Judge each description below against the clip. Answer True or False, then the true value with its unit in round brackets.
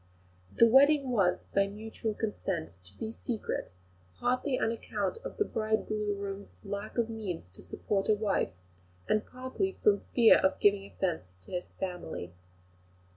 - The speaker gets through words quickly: False (145 wpm)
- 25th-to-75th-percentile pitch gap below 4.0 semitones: True (2.9 semitones)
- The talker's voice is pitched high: True (210 Hz)